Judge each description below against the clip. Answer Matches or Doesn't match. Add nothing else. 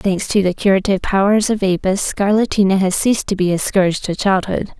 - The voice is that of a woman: Matches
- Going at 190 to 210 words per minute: Matches